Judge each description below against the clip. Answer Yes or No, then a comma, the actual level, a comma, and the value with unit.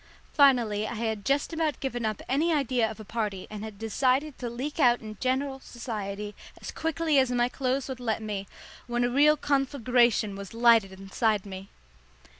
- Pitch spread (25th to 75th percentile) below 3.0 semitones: No, average, 4.1 semitones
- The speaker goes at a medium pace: Yes, average, 180 wpm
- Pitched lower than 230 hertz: No, high, 240 Hz